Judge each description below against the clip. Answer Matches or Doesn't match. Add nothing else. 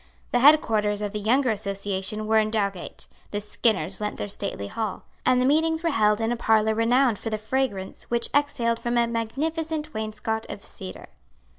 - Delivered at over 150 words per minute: Matches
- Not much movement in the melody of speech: Doesn't match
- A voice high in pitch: Matches